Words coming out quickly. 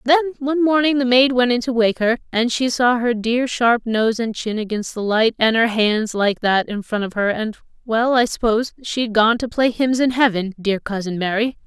Yes: fast, 215 wpm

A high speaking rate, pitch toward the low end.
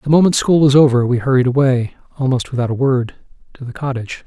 Yes: fast, 210 wpm; low, 130 Hz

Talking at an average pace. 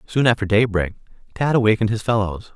Yes: average, 165 wpm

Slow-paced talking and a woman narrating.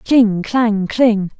Yes: slow, 130 wpm; female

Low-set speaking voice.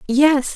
No: very high, 275 Hz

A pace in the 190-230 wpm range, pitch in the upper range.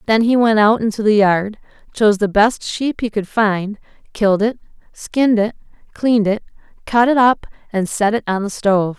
Yes: average, 195 wpm; high, 215 Hz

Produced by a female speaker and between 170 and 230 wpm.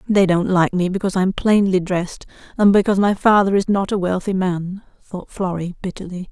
Yes: female; average, 200 wpm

